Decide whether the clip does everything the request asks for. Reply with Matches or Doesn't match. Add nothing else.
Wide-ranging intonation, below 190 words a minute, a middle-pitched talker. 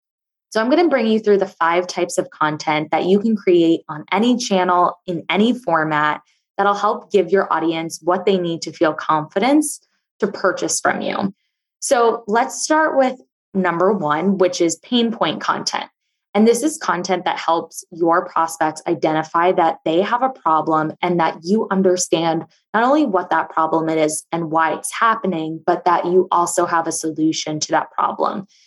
Doesn't match